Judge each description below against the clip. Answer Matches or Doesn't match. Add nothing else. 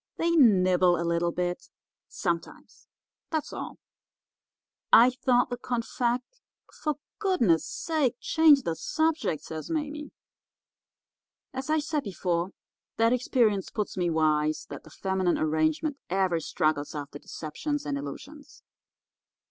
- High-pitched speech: Matches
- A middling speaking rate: Doesn't match